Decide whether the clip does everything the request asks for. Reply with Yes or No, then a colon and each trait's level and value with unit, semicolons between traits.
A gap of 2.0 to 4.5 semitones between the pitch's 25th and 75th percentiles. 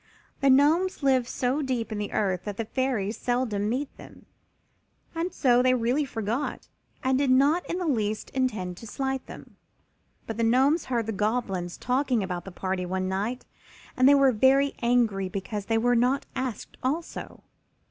Yes: average, 4.2 semitones